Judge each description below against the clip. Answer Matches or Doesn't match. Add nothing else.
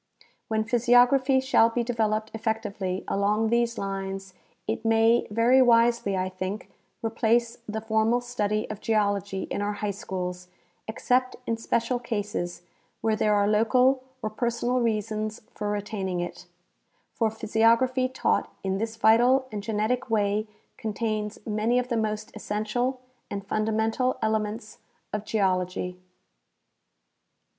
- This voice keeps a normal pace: Doesn't match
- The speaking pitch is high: Matches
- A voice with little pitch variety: Matches